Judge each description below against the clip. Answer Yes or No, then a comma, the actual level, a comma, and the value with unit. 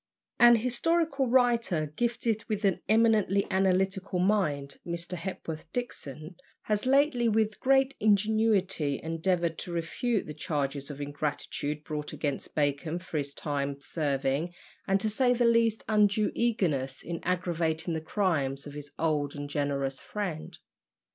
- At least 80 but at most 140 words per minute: Yes, slow, 135 wpm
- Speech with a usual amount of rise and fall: No, wide, 6.6 semitones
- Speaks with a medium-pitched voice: Yes, medium, 180 Hz